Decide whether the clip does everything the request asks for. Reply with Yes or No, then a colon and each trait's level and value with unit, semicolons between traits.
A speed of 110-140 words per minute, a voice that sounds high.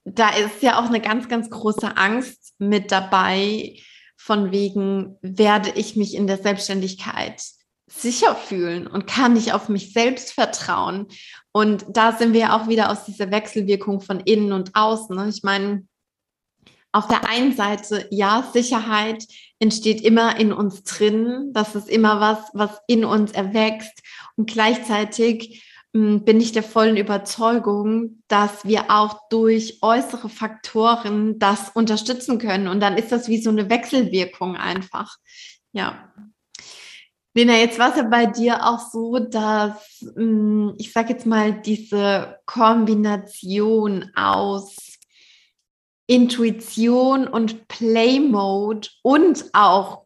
Yes: average, 130 wpm; high, 215 Hz